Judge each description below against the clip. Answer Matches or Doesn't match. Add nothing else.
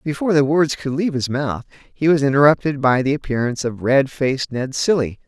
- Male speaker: Matches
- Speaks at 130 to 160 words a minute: Doesn't match